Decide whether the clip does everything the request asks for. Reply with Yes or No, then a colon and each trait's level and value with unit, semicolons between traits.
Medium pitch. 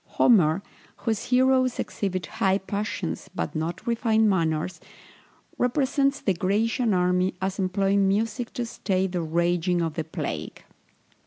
No: high, 195 Hz